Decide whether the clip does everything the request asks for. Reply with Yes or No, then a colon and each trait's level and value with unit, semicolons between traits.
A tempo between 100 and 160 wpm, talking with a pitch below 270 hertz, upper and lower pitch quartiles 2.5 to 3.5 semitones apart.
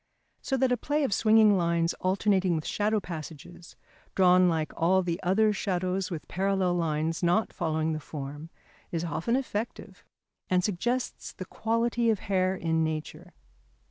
No: average, 150 wpm; medium, 185 Hz; average, 4.2 semitones